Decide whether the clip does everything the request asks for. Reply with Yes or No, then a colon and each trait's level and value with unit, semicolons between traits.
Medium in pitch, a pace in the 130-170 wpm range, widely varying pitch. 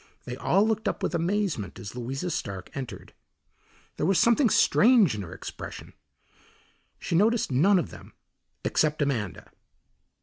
Yes: medium, 160 Hz; average, 140 wpm; wide, 9.0 semitones